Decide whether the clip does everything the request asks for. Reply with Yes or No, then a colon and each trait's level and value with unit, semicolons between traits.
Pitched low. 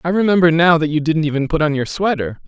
No: medium, 160 Hz